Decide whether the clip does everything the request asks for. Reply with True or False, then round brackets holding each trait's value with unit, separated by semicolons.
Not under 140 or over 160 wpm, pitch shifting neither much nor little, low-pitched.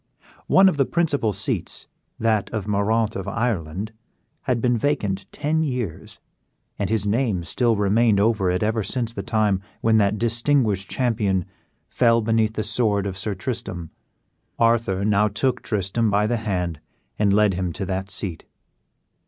True (155 wpm; 3.0 semitones; 110 Hz)